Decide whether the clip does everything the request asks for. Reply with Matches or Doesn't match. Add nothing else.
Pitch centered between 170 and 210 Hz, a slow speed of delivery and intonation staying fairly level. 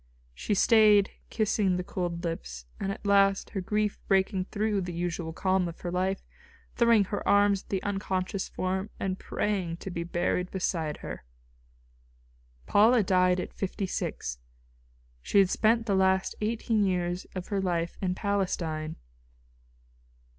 Doesn't match